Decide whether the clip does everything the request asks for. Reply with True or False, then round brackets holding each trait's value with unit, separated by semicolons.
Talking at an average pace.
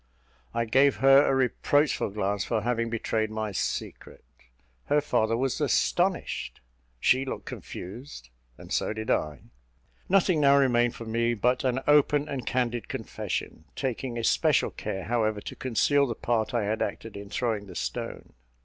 True (155 wpm)